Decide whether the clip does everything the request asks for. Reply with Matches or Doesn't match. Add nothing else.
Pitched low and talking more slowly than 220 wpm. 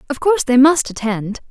Doesn't match